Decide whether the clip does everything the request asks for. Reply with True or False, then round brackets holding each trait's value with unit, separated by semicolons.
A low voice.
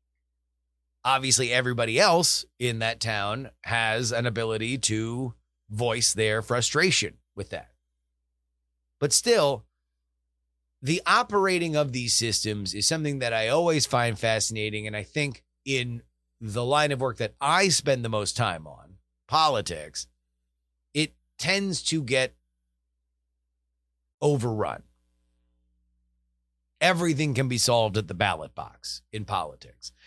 True (110 Hz)